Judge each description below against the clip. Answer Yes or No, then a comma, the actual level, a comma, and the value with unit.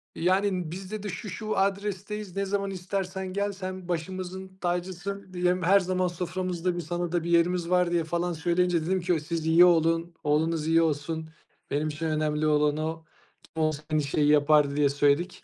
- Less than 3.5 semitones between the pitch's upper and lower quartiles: Yes, average, 2.8 semitones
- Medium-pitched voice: Yes, medium, 175 Hz